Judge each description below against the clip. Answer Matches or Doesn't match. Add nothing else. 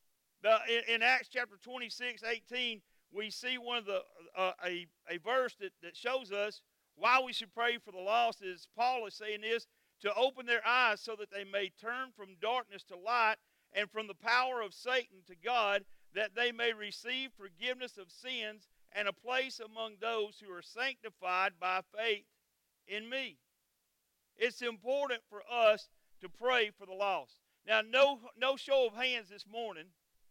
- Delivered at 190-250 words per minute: Doesn't match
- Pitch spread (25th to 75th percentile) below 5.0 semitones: Matches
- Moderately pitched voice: Doesn't match